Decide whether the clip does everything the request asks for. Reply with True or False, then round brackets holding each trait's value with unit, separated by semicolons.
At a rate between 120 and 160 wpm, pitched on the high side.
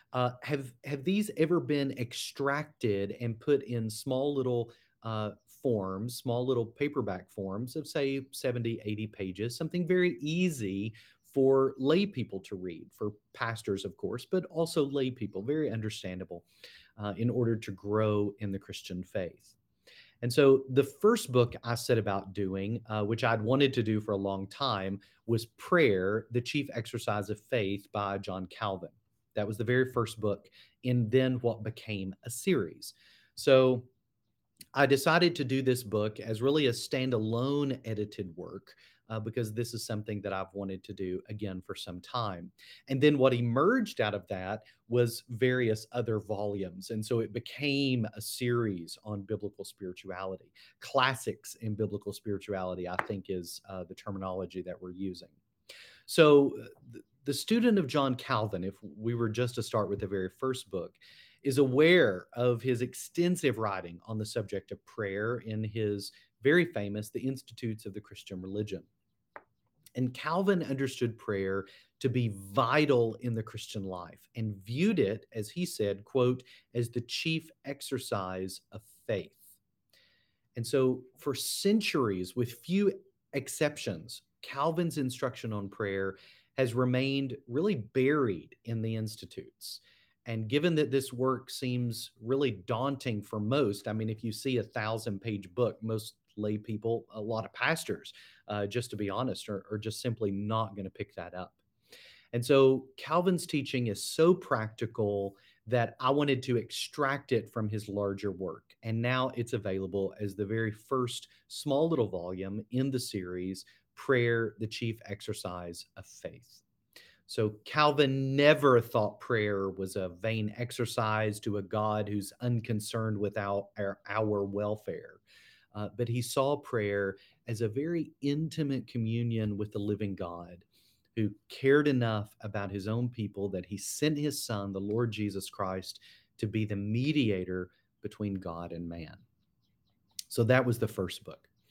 False (155 wpm; 115 Hz)